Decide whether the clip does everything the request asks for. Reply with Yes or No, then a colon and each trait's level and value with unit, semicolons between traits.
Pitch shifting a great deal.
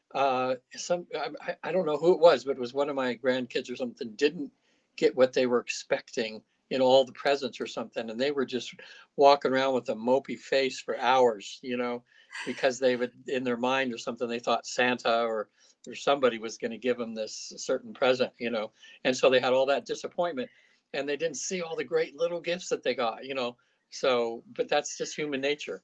Yes: wide, 5.7 semitones